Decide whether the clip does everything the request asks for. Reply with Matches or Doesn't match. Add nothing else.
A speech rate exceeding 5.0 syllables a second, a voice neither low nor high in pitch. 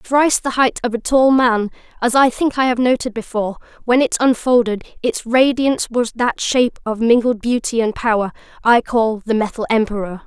Doesn't match